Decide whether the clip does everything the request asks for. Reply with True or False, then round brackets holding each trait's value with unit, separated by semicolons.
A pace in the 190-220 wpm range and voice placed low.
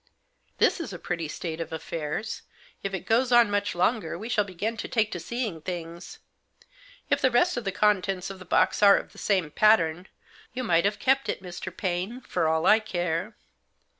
False (195 wpm; 195 Hz)